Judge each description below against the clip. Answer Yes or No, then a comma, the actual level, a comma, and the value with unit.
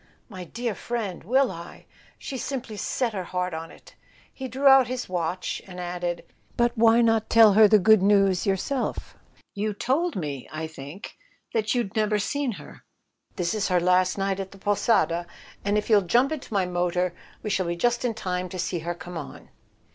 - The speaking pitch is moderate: No, high, 200 Hz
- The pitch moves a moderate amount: Yes, average, 4.5 semitones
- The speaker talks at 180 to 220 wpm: Yes, average, 185 wpm